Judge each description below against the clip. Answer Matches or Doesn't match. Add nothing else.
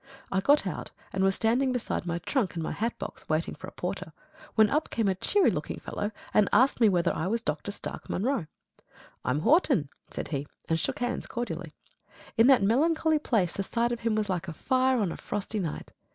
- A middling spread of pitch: Doesn't match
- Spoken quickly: Matches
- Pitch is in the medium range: Doesn't match